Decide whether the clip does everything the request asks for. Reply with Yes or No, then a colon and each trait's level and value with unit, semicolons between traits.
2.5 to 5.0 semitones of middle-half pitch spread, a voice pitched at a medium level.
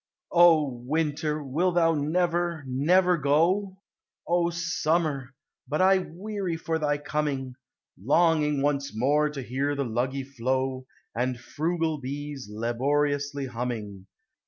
Yes: average, 3.9 semitones; medium, 145 Hz